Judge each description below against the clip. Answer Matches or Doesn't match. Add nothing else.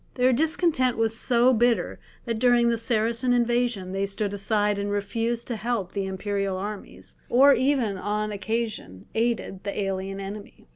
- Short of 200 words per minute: Matches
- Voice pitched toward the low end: Doesn't match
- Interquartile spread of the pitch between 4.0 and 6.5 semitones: Doesn't match